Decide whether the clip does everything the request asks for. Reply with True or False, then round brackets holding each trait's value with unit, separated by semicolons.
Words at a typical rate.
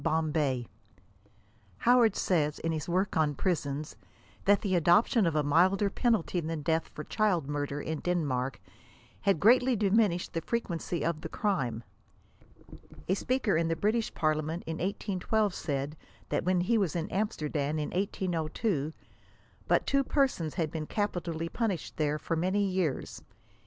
True (150 wpm)